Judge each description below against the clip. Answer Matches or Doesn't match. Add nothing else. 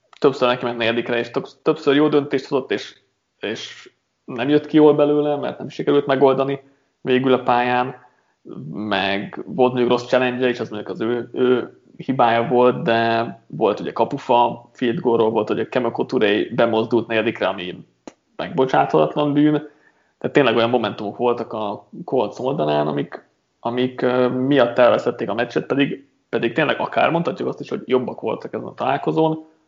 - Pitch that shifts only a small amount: Doesn't match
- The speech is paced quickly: Matches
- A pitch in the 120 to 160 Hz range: Matches